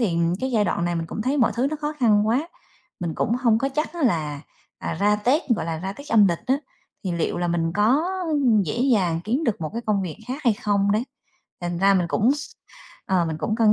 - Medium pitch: No, high, 210 Hz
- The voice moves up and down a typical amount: No, wide, 6.1 semitones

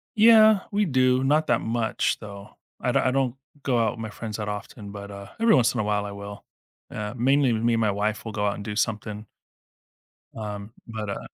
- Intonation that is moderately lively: Yes, average, 3.6 semitones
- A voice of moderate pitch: No, low, 110 Hz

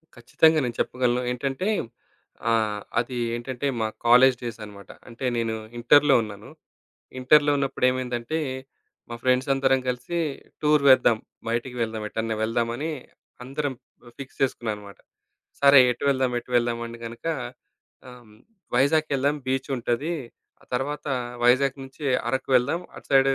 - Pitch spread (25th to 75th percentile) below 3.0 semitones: Yes, narrow, 2.6 semitones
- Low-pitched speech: Yes, low, 125 Hz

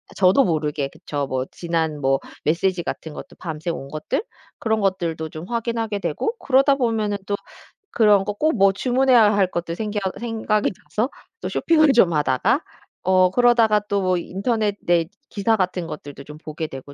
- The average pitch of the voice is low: No, high, 195 Hz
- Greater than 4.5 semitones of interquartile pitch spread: Yes, wide, 5.5 semitones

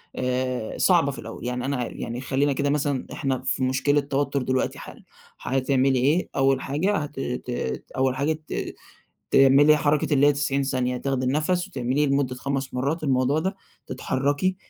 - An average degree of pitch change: No, narrow, 2.1 semitones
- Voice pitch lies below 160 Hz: Yes, low, 135 Hz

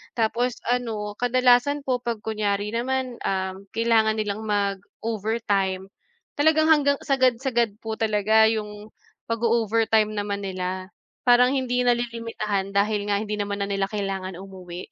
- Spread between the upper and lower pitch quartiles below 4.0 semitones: Yes, average, 3.1 semitones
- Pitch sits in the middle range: No, high, 220 Hz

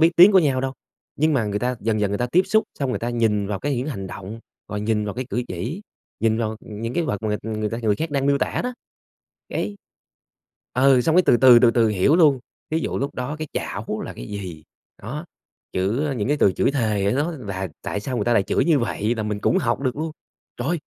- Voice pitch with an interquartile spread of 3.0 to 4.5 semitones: No, average, 5.1 semitones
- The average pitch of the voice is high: No, low, 120 Hz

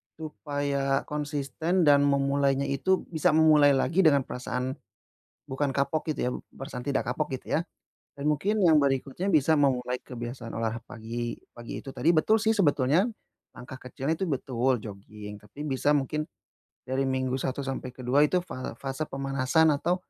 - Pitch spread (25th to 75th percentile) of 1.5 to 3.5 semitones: Yes, average, 3.0 semitones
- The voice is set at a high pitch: No, medium, 140 Hz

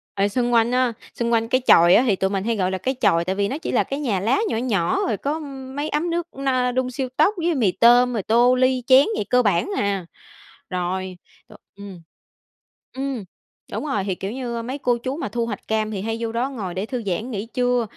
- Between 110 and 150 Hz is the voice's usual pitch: No, high, 235 Hz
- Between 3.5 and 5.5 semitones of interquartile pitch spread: Yes, average, 4.3 semitones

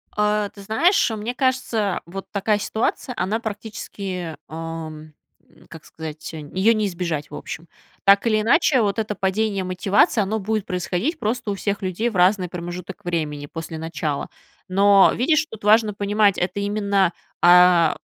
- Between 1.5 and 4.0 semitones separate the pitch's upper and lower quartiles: Yes, average, 3.5 semitones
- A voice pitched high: Yes, high, 200 Hz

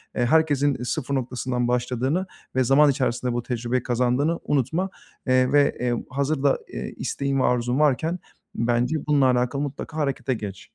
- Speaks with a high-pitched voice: No, low, 130 Hz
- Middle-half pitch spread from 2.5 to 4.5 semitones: Yes, average, 2.8 semitones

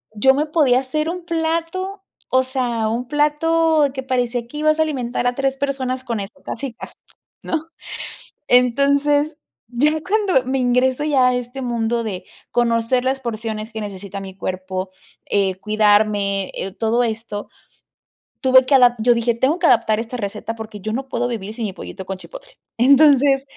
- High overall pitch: Yes, very high, 250 Hz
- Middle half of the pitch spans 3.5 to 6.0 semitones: Yes, average, 4.2 semitones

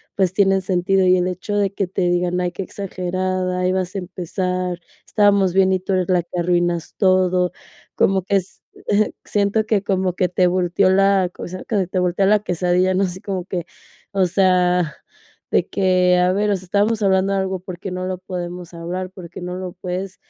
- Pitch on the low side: No, medium, 185 Hz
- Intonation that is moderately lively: No, narrow, 1.3 semitones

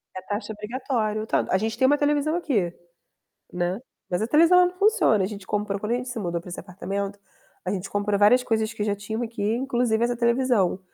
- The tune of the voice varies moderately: Yes, average, 3.7 semitones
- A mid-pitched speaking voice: No, high, 220 Hz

